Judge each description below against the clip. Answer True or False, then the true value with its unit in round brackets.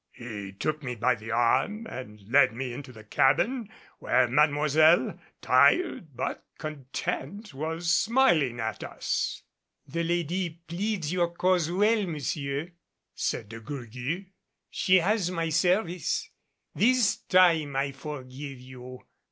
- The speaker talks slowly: True (125 wpm)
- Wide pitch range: True (5.9 semitones)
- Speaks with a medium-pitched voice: True (155 Hz)